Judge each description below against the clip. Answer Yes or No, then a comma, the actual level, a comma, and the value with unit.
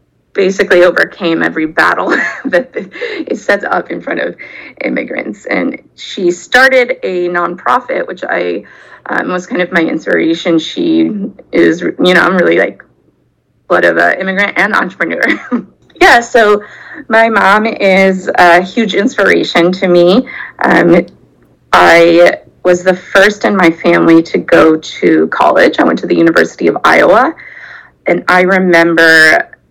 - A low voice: No, medium, 185 Hz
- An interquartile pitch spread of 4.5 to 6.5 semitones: Yes, average, 4.8 semitones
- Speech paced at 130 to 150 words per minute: Yes, average, 140 wpm